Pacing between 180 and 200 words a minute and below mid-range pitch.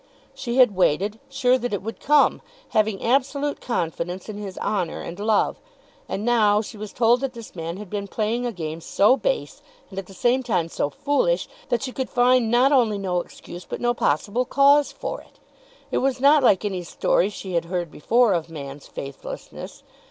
No: average, 195 wpm; high, 215 Hz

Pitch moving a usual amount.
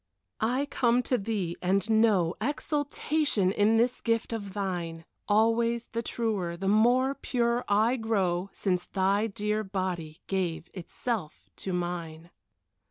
Yes: average, 4.3 semitones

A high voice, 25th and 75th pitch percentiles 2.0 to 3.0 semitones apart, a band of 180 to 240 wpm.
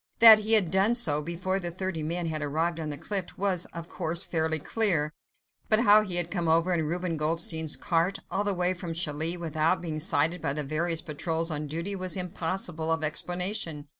No: medium, 170 Hz; average, 2.7 semitones; average, 200 wpm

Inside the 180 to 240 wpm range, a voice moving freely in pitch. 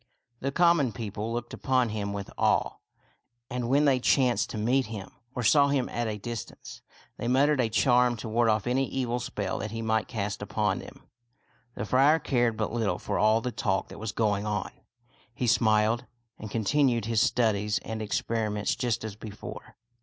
No: average, 185 wpm; average, 2.9 semitones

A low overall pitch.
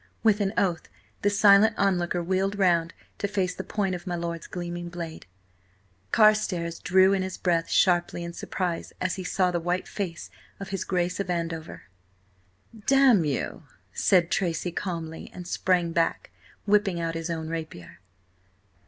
No: medium, 180 Hz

